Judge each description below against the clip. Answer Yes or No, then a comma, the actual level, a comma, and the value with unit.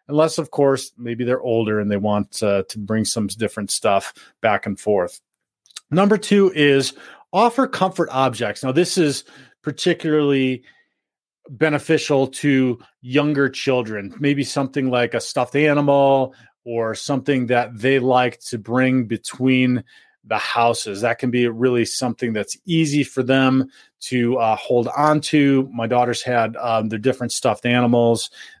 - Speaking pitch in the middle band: No, low, 130 Hz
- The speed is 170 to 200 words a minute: No, average, 145 wpm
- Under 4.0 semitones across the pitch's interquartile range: Yes, average, 3.4 semitones